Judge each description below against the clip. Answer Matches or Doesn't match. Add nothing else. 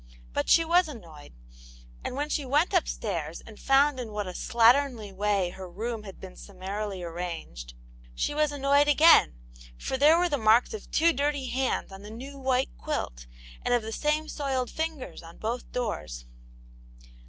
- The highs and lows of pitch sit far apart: Matches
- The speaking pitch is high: Matches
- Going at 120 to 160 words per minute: Doesn't match